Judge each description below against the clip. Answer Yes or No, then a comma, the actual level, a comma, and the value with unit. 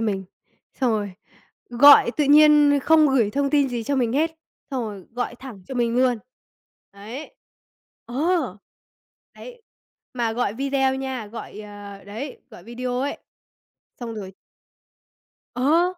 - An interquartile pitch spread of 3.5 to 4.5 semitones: Yes, average, 4.2 semitones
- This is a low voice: No, very high, 250 Hz